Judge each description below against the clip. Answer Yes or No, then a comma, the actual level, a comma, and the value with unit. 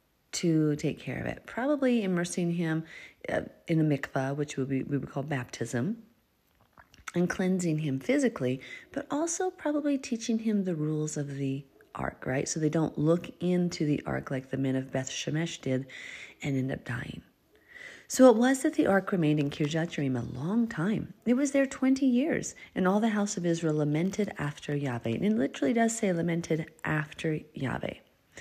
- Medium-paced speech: Yes, average, 180 wpm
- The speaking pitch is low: No, medium, 165 Hz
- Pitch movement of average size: No, wide, 7.5 semitones